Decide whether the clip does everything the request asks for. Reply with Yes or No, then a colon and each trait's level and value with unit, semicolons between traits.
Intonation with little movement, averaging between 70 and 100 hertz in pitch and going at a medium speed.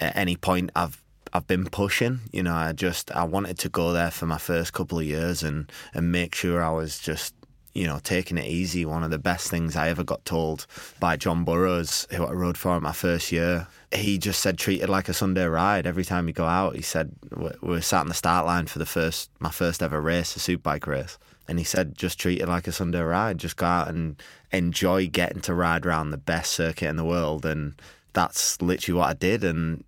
No: narrow, 1.9 semitones; very low, 85 Hz; fast, 240 wpm